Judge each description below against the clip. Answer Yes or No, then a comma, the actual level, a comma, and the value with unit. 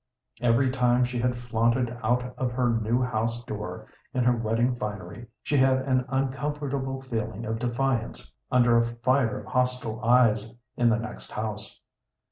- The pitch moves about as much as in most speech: No, narrow, 2.0 semitones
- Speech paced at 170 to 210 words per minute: No, average, 155 wpm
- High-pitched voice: No, low, 120 Hz